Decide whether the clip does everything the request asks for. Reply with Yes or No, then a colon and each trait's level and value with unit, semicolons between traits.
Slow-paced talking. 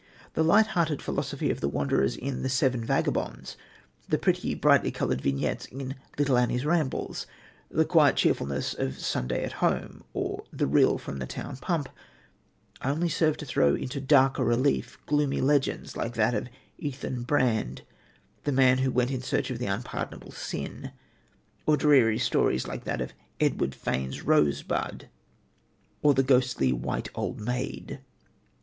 No: average, 155 wpm